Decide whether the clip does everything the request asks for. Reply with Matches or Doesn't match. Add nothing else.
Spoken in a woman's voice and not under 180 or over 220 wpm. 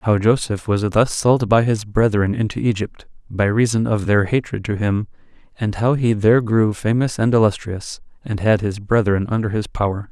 Doesn't match